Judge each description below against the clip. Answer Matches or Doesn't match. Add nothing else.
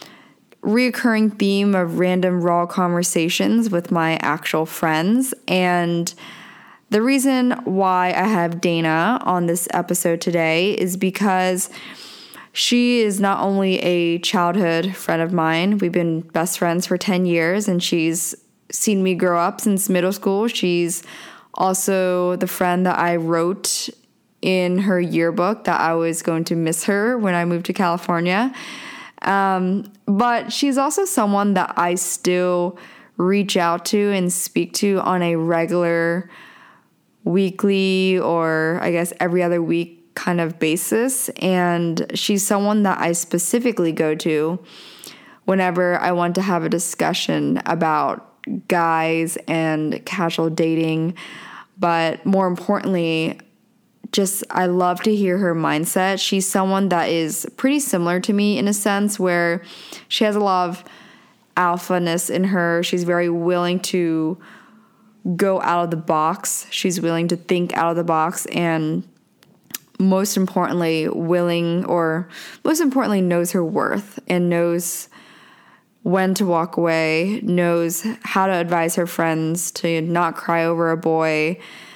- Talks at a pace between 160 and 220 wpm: Doesn't match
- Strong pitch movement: Doesn't match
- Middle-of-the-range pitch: Matches